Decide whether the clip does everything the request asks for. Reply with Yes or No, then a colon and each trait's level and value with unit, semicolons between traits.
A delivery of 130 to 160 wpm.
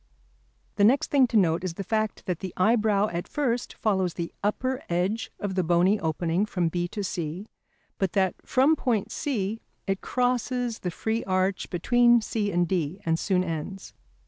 No: average, 175 wpm